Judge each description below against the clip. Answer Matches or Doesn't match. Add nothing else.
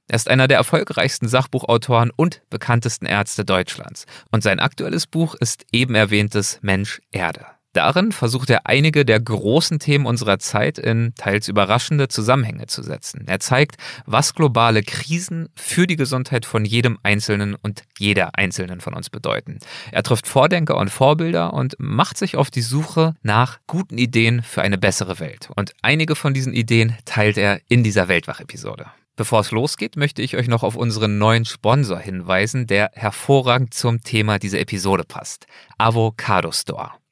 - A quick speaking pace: Doesn't match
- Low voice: Matches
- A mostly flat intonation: Doesn't match